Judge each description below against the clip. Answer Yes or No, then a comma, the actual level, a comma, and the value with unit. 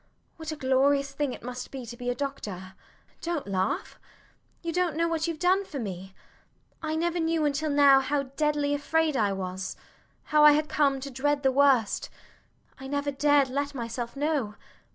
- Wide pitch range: No, average, 3.2 semitones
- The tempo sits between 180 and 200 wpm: Yes, average, 190 wpm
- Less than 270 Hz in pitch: No, very high, 280 Hz